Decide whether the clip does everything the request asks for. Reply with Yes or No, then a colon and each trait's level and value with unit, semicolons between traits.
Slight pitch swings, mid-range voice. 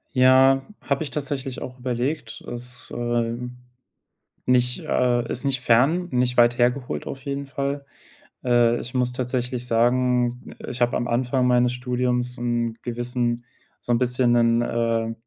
No: narrow, 1.2 semitones; low, 125 Hz